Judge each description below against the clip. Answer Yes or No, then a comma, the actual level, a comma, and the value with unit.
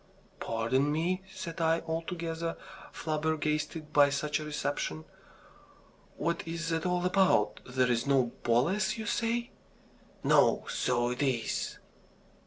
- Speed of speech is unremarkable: No, slow, 115 wpm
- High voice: No, medium, 155 Hz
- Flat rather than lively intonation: No, average, 3.7 semitones